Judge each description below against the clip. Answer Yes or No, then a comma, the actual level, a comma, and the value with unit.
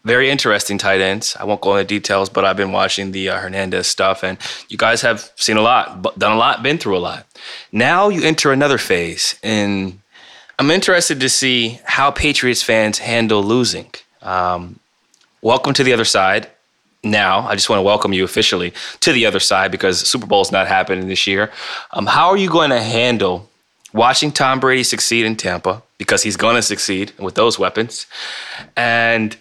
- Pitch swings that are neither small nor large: Yes, average, 4.2 semitones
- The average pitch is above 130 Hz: No, low, 105 Hz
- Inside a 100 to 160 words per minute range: No, average, 190 wpm